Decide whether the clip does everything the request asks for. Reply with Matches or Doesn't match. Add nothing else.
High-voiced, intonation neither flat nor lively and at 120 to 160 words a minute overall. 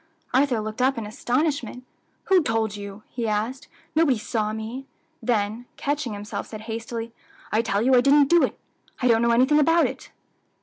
Doesn't match